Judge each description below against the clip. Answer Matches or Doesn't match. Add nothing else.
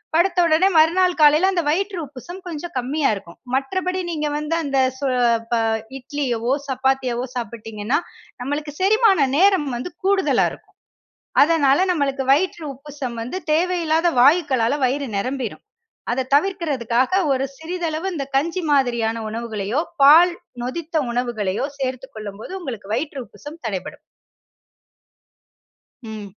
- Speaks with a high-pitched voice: Matches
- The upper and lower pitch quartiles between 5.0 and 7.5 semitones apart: Matches